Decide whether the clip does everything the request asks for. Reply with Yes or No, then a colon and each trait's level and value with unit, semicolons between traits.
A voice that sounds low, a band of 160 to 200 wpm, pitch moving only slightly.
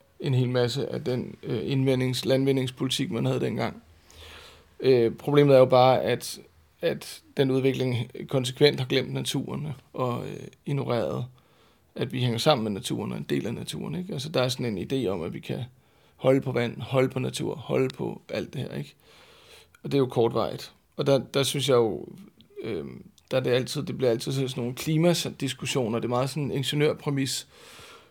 Yes: low, 130 Hz; average, 185 wpm; narrow, 2.3 semitones